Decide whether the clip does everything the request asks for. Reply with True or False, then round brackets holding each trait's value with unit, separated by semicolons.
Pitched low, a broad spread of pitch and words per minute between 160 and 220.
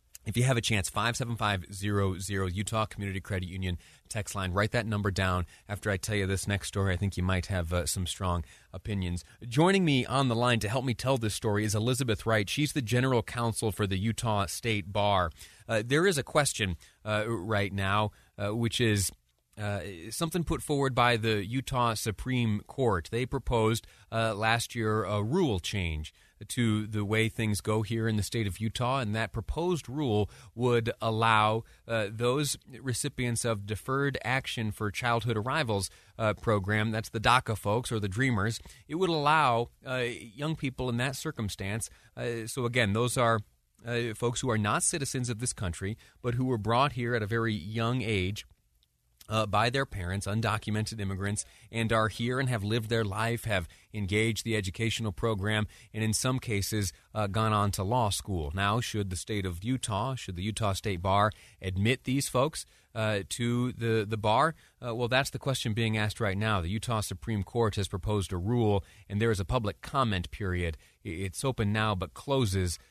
False (110 Hz; 3.2 semitones; 190 wpm)